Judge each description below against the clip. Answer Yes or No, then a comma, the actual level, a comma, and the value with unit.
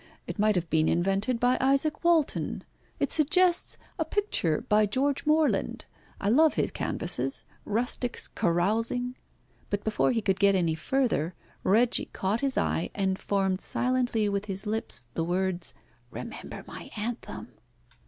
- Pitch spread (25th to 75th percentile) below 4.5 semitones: No, average, 5.1 semitones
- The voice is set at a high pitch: Yes, high, 215 Hz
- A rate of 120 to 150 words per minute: Yes, average, 145 wpm